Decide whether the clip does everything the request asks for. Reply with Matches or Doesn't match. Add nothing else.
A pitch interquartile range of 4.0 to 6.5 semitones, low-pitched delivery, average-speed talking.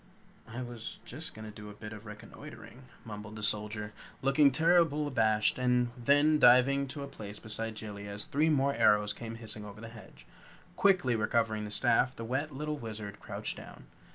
Matches